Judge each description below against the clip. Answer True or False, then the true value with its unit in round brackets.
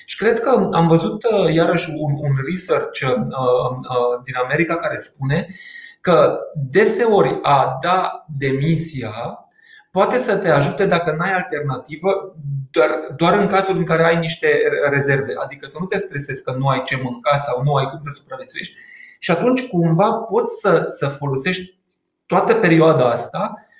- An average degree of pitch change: False (6.2 semitones)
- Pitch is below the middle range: False (165 Hz)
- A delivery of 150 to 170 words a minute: True (155 wpm)